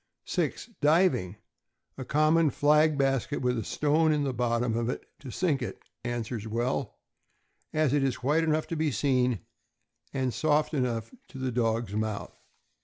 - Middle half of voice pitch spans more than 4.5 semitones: No, average, 4.2 semitones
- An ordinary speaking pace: Yes, average, 160 wpm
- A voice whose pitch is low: Yes, low, 130 Hz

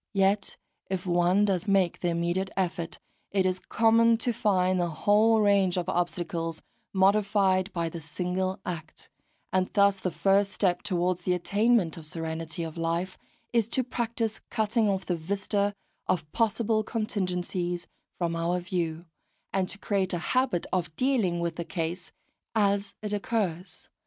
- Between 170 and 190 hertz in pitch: Yes, medium, 185 Hz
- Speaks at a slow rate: No, average, 150 wpm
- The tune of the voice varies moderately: Yes, average, 3.0 semitones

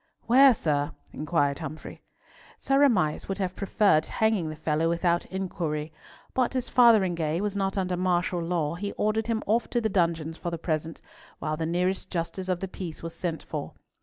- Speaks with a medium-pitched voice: Yes, medium, 175 Hz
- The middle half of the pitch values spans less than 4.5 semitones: Yes, average, 3.8 semitones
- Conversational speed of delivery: Yes, average, 180 wpm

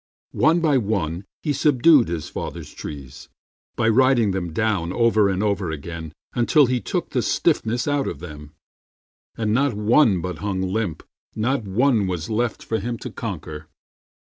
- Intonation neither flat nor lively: No, wide, 5.7 semitones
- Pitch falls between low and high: No, low, 105 Hz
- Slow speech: No, average, 160 wpm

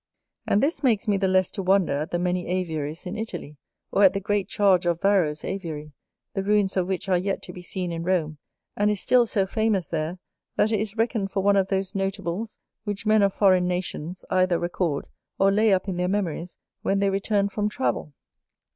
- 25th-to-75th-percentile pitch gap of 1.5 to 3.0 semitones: Yes, narrow, 2.4 semitones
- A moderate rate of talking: No, fast, 210 wpm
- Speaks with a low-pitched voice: No, high, 190 Hz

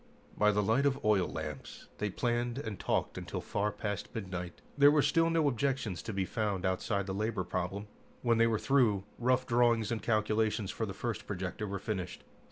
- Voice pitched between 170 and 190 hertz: No, low, 110 Hz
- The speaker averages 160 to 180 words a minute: No, average, 190 wpm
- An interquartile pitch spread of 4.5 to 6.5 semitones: No, average, 3.5 semitones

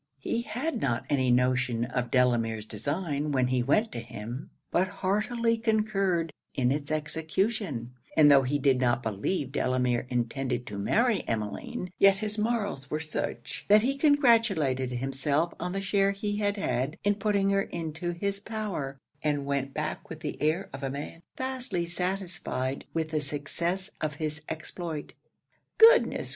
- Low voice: No, medium, 155 Hz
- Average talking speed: Yes, average, 155 wpm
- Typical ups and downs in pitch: No, wide, 7.2 semitones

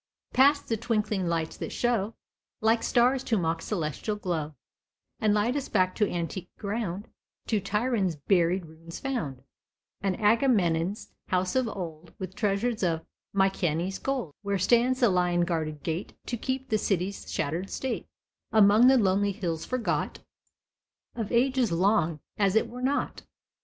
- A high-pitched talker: Yes, high, 200 Hz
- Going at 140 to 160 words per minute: Yes, average, 145 wpm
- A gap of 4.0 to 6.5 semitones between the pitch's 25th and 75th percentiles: Yes, average, 5.0 semitones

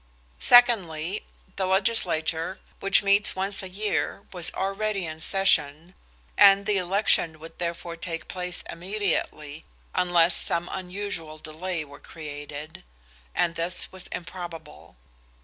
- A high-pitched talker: No, medium, 180 Hz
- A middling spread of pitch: Yes, average, 3.2 semitones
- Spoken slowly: Yes, slow, 115 wpm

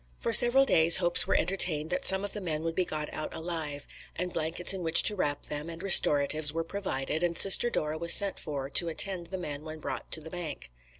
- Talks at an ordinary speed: No, fast, 225 wpm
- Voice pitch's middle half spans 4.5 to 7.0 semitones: No, average, 3.4 semitones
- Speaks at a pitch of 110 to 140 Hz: No, medium, 165 Hz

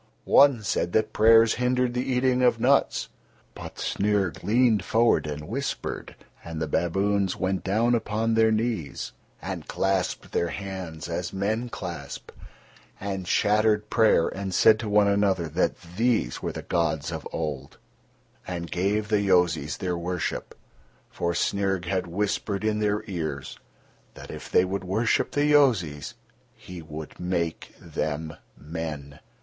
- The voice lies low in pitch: Yes, very low, 95 Hz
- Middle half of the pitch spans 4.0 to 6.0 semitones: Yes, average, 4.4 semitones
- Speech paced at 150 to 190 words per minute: No, average, 140 wpm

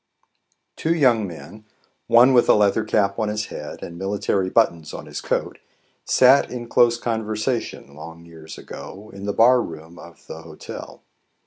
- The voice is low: Yes, low, 105 Hz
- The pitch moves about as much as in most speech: No, wide, 5.7 semitones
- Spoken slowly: No, average, 160 wpm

